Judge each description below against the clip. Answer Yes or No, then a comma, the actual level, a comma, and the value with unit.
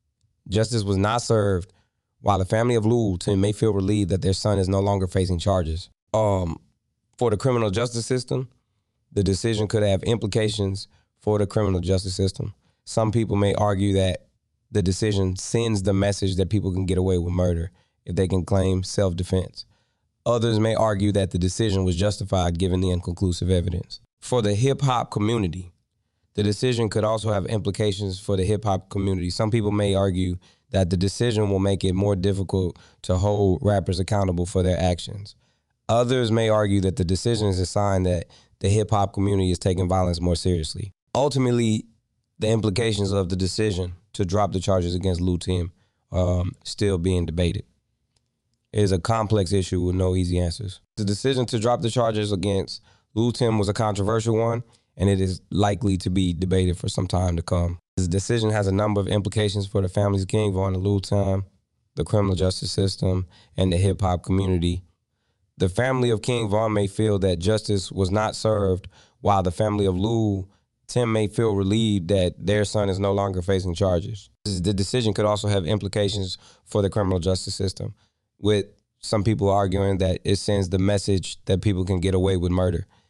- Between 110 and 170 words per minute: No, average, 185 wpm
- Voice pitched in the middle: No, low, 100 Hz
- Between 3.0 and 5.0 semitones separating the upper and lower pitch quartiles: No, narrow, 2.5 semitones